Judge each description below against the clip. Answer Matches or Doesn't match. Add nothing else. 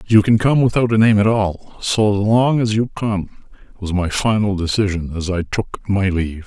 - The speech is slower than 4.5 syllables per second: Doesn't match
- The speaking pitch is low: Matches